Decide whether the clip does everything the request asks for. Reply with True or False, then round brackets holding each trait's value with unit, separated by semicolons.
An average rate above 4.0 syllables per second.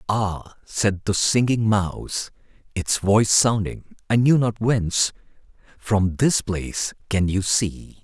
False (3.9 syllables/s)